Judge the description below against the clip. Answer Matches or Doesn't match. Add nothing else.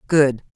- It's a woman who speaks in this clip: Matches